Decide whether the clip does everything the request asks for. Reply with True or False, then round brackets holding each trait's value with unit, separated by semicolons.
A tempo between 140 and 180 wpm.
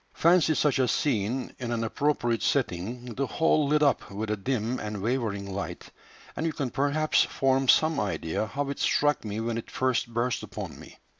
False (190 wpm)